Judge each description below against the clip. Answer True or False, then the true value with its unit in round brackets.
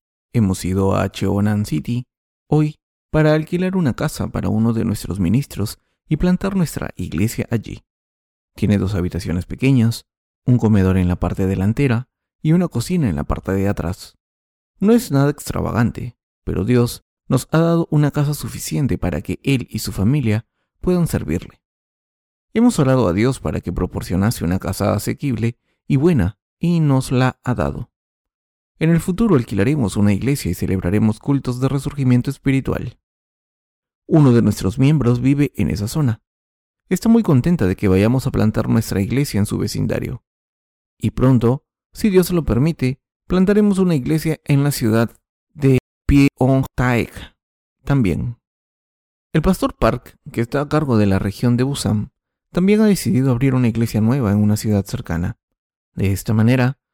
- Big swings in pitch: True (6.2 semitones)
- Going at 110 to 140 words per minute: False (155 wpm)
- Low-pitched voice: True (120 Hz)